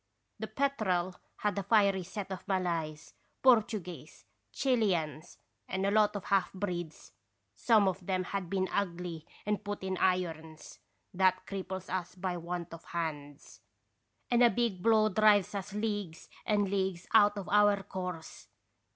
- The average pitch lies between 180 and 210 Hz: Yes, high, 190 Hz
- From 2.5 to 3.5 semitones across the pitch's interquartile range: Yes, average, 2.8 semitones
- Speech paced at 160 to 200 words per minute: No, average, 150 wpm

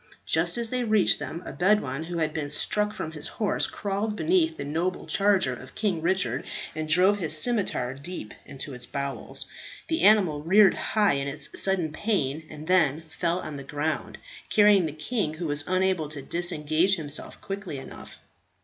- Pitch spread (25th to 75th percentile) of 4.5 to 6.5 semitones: Yes, average, 5.1 semitones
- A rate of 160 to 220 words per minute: Yes, average, 175 wpm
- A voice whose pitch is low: No, medium, 170 Hz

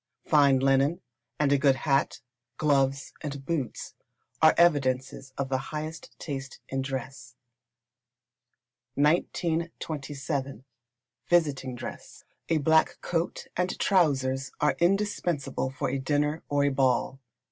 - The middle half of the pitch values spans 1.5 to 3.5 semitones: Yes, average, 2.8 semitones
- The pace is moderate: No, slow, 115 wpm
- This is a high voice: No, medium, 140 Hz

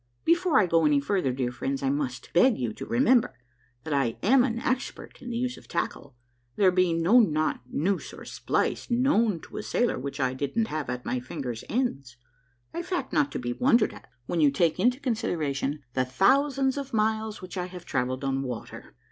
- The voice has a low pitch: No, medium, 180 Hz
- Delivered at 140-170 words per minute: No, average, 200 wpm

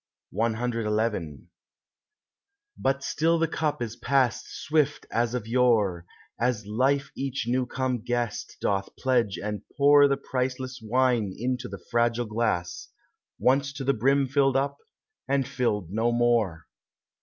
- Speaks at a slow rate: Yes, slow, 130 wpm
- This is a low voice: Yes, low, 120 Hz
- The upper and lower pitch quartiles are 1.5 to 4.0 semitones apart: Yes, average, 3.5 semitones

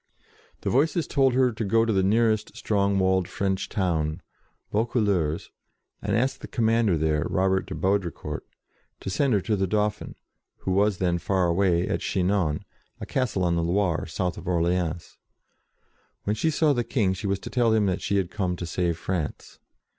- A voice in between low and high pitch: No, very low, 95 Hz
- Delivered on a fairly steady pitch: No, average, 3.7 semitones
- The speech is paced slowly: No, average, 180 wpm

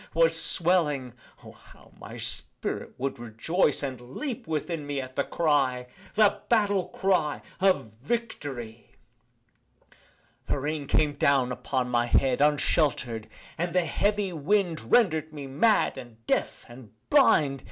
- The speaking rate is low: Yes, slow, 130 wpm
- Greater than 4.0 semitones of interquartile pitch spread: Yes, wide, 5.6 semitones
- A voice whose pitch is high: No, medium, 145 Hz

